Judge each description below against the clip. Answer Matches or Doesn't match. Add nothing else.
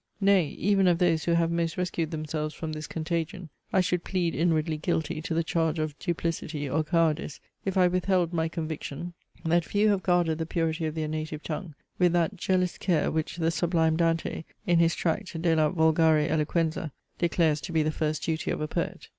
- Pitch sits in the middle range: Matches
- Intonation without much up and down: Matches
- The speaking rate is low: Doesn't match